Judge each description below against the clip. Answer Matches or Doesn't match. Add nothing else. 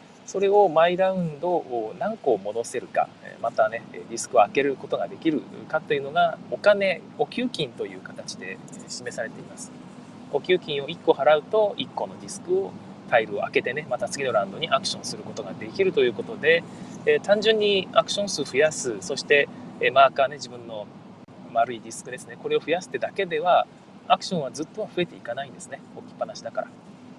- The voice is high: Matches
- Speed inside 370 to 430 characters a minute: Matches